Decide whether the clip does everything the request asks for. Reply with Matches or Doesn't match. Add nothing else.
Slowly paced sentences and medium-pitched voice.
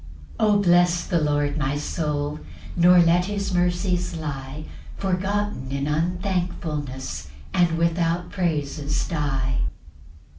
Matches